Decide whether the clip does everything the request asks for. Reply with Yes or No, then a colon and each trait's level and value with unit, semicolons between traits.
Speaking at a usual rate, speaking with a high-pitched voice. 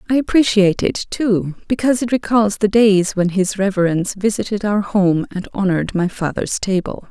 Yes: average, 170 wpm; high, 200 Hz